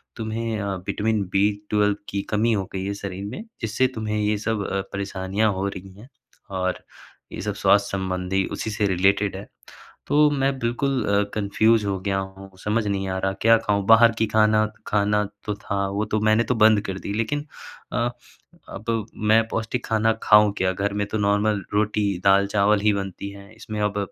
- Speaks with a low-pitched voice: Yes, low, 105 Hz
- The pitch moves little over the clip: Yes, narrow, 1.8 semitones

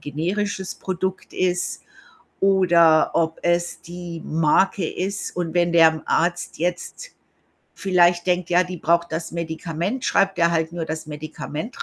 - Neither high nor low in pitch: Yes, medium, 175 Hz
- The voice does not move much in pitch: Yes, narrow, 2.1 semitones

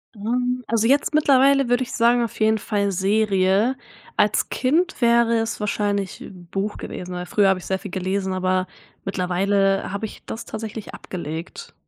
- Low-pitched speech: No, high, 210 Hz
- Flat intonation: No, average, 3.8 semitones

